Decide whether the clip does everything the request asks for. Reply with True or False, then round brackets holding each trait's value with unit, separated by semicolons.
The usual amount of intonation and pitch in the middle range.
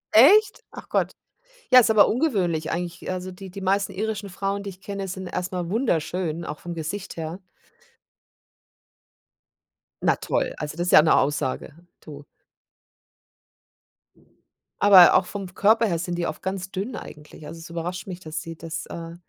True (3.1 semitones; 180 Hz)